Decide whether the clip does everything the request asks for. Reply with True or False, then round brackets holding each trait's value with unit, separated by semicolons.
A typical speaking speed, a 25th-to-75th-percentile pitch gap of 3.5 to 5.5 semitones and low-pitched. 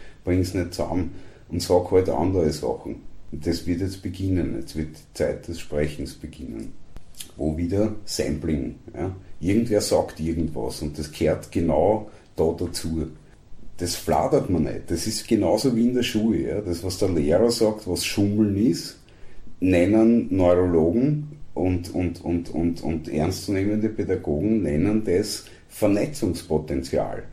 True (145 wpm; 4.1 semitones; 90 Hz)